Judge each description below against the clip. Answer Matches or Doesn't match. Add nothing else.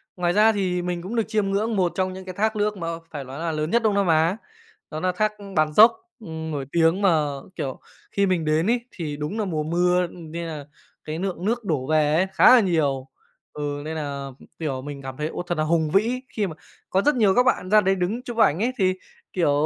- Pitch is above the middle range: Doesn't match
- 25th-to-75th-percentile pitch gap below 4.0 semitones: Doesn't match